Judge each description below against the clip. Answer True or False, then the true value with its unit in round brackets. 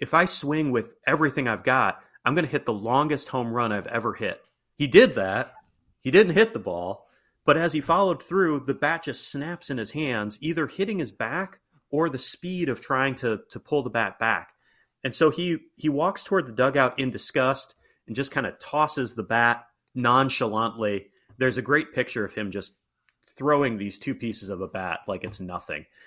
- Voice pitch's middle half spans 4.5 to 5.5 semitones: True (5.1 semitones)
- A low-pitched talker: True (130 Hz)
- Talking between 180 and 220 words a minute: True (200 wpm)